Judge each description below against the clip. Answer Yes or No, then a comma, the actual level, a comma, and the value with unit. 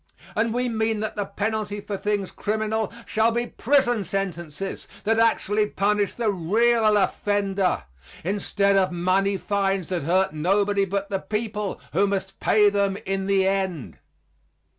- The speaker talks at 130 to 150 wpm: Yes, average, 145 wpm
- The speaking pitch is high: Yes, high, 200 Hz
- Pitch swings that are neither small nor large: No, narrow, 1.9 semitones